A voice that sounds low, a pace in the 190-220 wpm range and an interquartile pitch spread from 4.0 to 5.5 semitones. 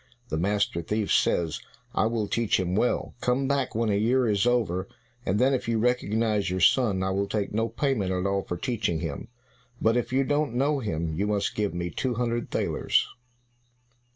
Yes: low, 105 Hz; average, 195 wpm; average, 4.3 semitones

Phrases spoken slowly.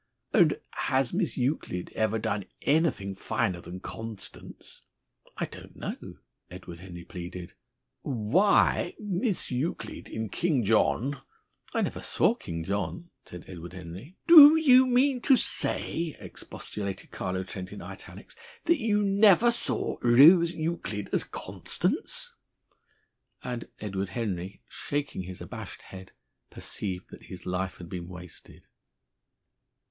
Yes: slow, 125 wpm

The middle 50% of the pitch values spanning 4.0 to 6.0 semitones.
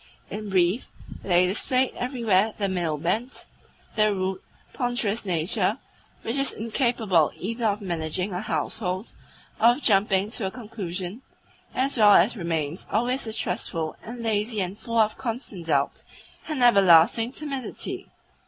Yes: average, 4.4 semitones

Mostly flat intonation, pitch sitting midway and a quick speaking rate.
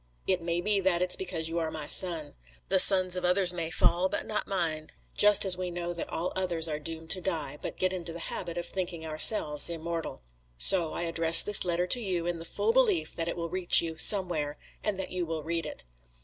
Yes: narrow, 2.1 semitones; medium, 175 Hz; fast, 230 wpm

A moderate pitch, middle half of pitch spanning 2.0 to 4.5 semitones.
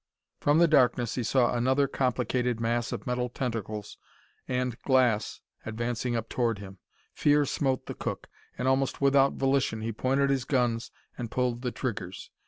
No: low, 125 Hz; narrow, 2.4 semitones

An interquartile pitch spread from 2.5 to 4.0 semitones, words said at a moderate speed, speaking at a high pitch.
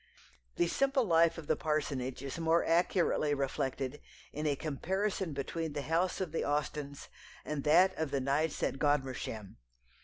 No: average, 3.2 semitones; average, 155 wpm; medium, 150 Hz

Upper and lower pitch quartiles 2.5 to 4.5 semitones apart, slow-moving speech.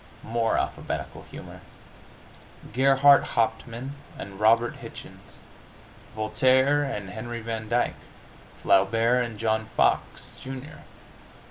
Yes: average, 3.0 semitones; slow, 95 wpm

